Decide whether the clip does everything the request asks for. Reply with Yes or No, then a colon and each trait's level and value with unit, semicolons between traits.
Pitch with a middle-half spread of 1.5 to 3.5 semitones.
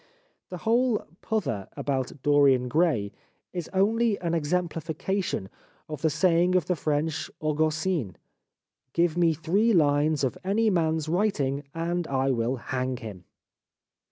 No: average, 4.6 semitones